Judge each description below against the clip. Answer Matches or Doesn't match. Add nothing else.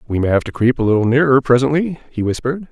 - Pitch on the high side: Doesn't match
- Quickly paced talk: Matches